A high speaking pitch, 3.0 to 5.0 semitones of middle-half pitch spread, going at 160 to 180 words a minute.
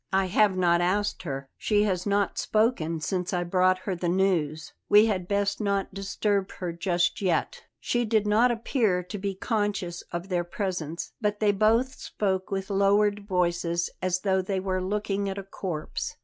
No: high, 195 Hz; narrow, 2.5 semitones; average, 175 wpm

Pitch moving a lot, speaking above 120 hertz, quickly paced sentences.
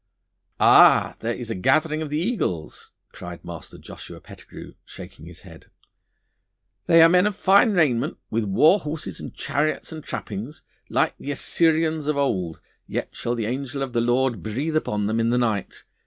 No: wide, 5.8 semitones; low, 135 Hz; average, 170 wpm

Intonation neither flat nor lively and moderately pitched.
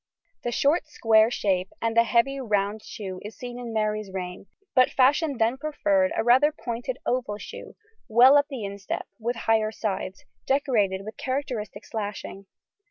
No: average, 4.0 semitones; high, 230 Hz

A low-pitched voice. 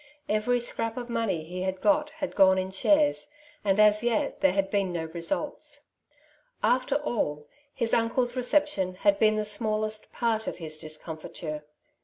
No: high, 215 Hz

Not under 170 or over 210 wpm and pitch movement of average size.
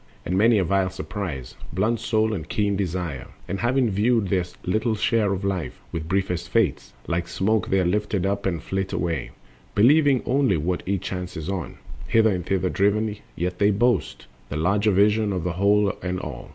Yes: average, 185 wpm; average, 3.0 semitones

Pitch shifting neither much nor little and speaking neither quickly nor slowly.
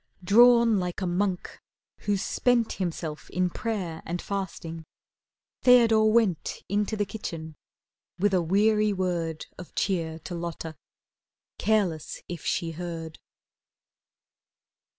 No: average, 4.1 semitones; slow, 110 wpm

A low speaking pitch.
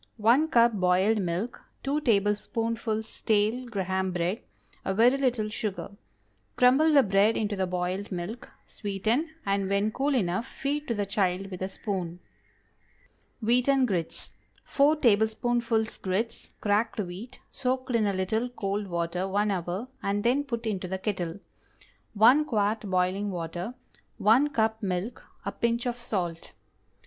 No: high, 210 Hz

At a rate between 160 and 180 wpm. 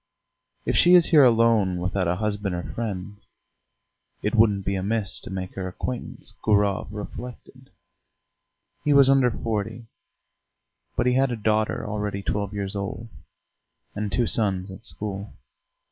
No: average, 145 wpm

